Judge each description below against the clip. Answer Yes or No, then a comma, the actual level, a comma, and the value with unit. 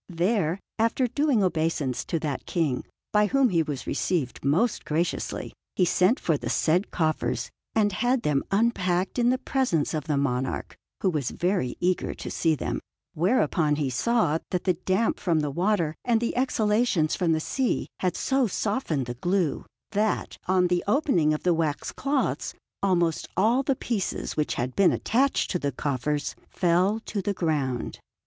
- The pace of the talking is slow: No, average, 170 wpm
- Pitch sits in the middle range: Yes, medium, 180 Hz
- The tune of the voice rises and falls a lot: Yes, wide, 6.0 semitones